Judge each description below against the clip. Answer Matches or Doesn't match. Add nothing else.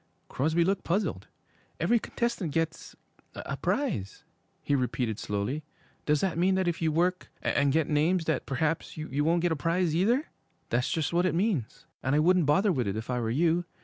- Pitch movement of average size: Matches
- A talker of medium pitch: Matches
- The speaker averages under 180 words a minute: Doesn't match